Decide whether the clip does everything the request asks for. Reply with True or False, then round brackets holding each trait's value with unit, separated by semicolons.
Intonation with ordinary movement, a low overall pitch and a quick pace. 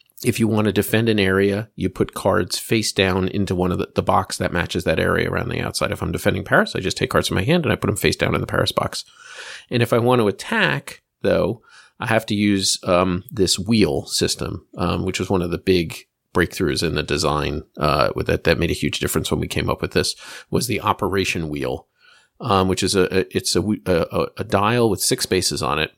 True (3.0 semitones; 95 Hz; 240 wpm)